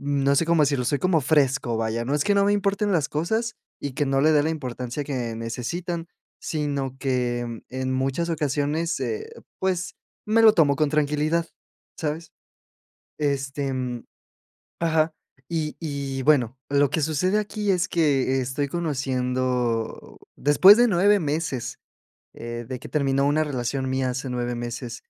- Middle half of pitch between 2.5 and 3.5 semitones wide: No, average, 4.1 semitones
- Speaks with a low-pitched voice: No, medium, 145 Hz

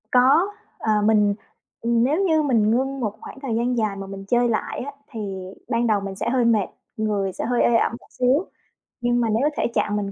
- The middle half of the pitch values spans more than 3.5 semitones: No, average, 3.1 semitones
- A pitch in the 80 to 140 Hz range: No, high, 235 Hz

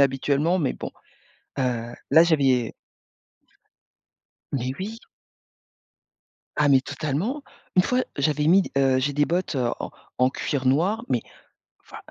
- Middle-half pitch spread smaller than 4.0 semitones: No, average, 4.7 semitones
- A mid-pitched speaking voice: Yes, medium, 145 Hz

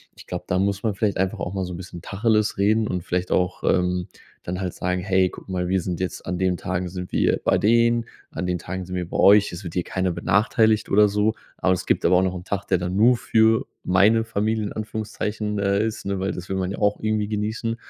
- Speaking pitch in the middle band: No, very low, 95 Hz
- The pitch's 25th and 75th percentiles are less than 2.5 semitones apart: No, average, 2.8 semitones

